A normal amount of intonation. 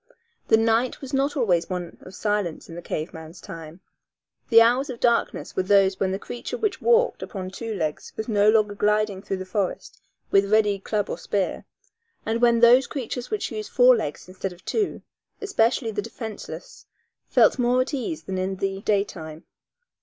Yes: average, 4.1 semitones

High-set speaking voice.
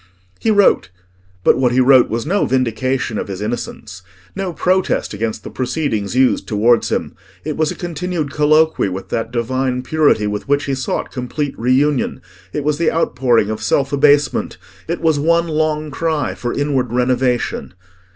No: low, 135 Hz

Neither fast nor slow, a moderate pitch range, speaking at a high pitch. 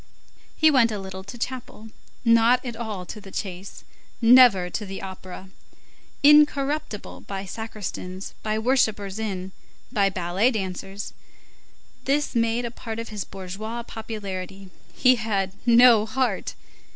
No: slow, 130 wpm; average, 3.6 semitones; high, 215 Hz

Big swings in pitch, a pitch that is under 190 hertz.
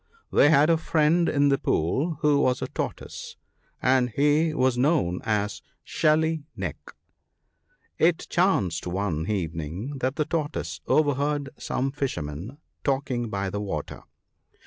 Yes: wide, 6.9 semitones; low, 135 Hz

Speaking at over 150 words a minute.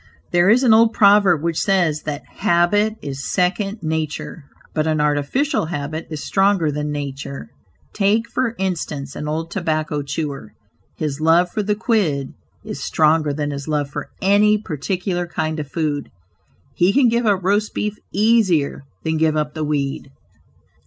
Yes: average, 160 wpm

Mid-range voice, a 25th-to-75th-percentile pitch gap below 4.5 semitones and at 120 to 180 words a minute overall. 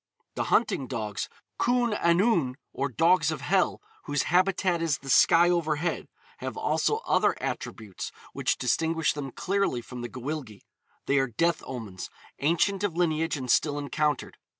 No: medium, 155 Hz; average, 4.9 semitones; average, 150 wpm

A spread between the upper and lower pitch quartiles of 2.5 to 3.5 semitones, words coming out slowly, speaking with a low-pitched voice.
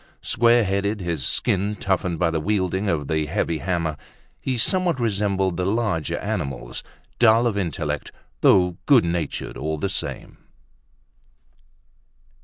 No: average, 4.5 semitones; slow, 130 wpm; very low, 95 Hz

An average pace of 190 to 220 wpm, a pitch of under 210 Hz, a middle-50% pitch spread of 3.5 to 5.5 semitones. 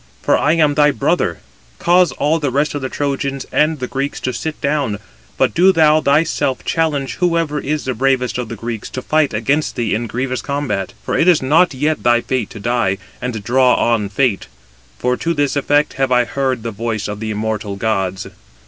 Yes: average, 200 wpm; low, 135 Hz; average, 4.3 semitones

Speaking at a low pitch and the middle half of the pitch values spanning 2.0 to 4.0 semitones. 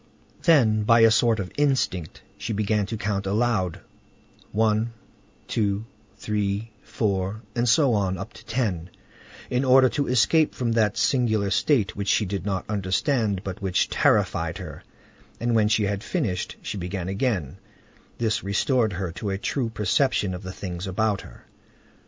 Yes: low, 105 Hz; average, 3.2 semitones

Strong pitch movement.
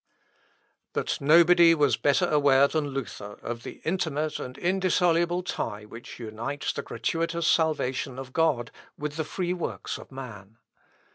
No: average, 4.8 semitones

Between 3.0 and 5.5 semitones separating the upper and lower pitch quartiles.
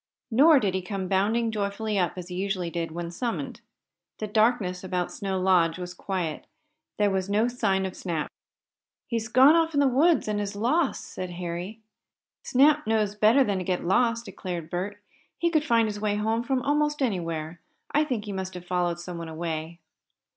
Yes: average, 4.6 semitones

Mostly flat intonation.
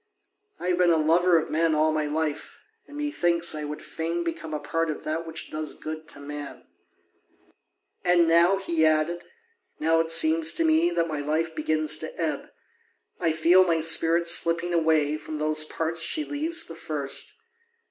Yes: narrow, 1.9 semitones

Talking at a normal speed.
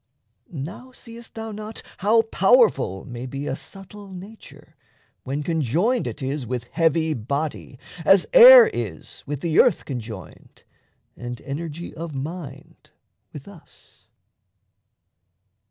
No: slow, 120 wpm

